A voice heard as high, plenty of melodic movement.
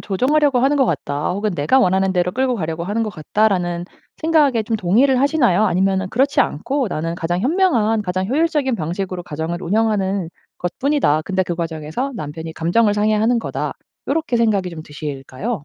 Yes: high, 200 Hz; wide, 6.4 semitones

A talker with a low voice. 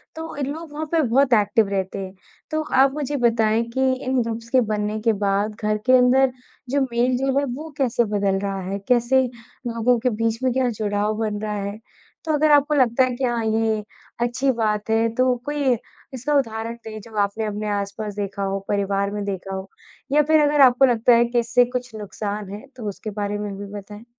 No: high, 230 Hz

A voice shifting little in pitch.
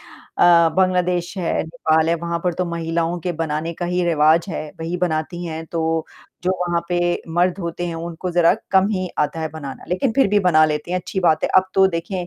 Yes: narrow, 1.8 semitones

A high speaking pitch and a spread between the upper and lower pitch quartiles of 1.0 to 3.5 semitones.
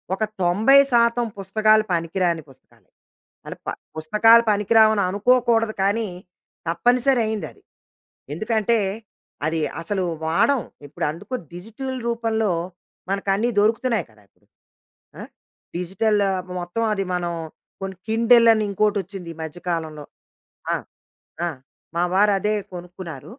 No: high, 205 Hz; average, 4.5 semitones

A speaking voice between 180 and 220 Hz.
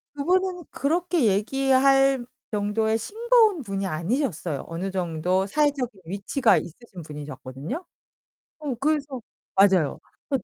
No: high, 230 Hz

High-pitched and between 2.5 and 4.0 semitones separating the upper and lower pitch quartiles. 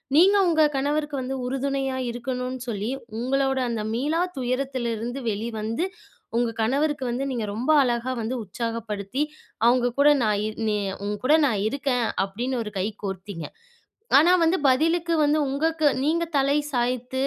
Yes: very high, 255 Hz; average, 3.5 semitones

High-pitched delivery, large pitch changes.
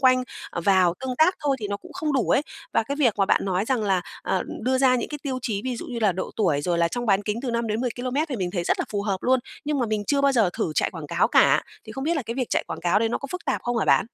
No: high, 235 Hz; average, 4.8 semitones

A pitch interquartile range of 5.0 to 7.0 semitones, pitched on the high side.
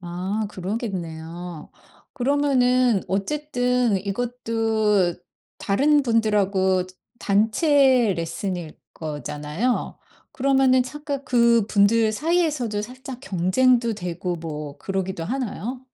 Yes: average, 5.3 semitones; high, 220 Hz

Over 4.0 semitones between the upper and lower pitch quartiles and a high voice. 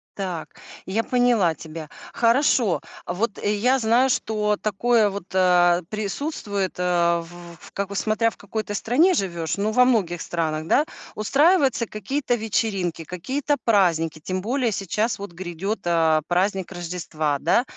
Yes: average, 4.8 semitones; high, 200 Hz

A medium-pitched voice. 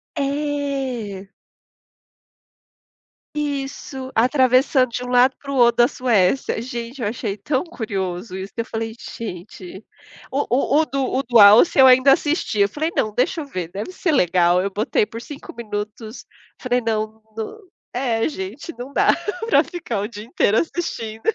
No: high, 240 Hz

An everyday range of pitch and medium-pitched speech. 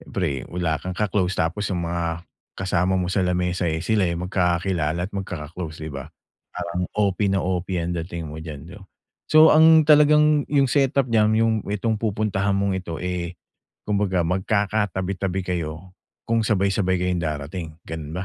No: average, 3.3 semitones; very low, 90 Hz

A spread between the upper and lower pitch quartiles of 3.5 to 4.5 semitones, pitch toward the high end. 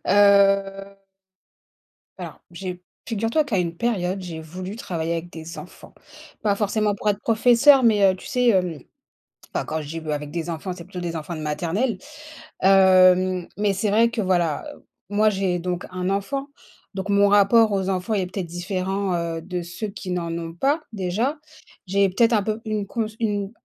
No: average, 3.0 semitones; high, 195 Hz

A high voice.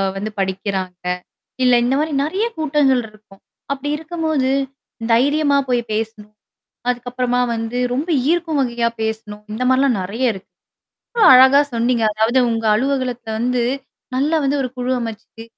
Yes: very high, 250 Hz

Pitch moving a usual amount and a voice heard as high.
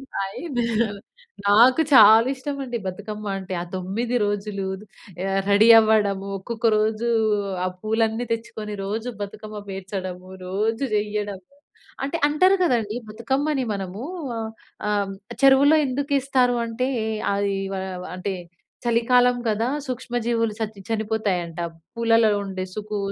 Yes: average, 3.5 semitones; high, 220 Hz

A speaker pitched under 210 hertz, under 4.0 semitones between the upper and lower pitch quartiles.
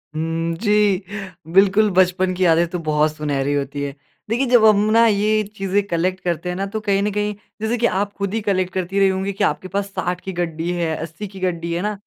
Yes: medium, 185 Hz; average, 3.3 semitones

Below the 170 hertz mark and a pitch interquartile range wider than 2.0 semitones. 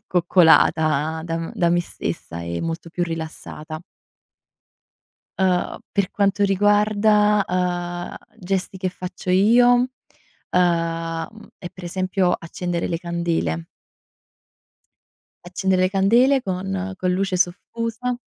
No: medium, 185 Hz; narrow, 2.6 semitones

